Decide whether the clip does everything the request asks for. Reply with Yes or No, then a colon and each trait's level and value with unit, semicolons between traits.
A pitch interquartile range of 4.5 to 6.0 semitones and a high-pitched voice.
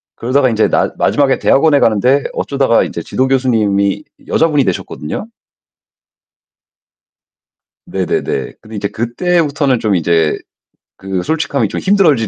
No: wide, 5.6 semitones; low, 125 Hz